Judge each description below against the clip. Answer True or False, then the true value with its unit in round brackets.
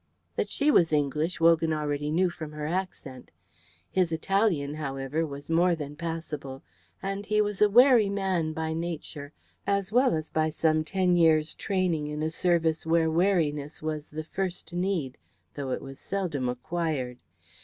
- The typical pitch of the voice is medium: True (160 Hz)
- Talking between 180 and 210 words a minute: False (160 wpm)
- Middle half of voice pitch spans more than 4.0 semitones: False (3.5 semitones)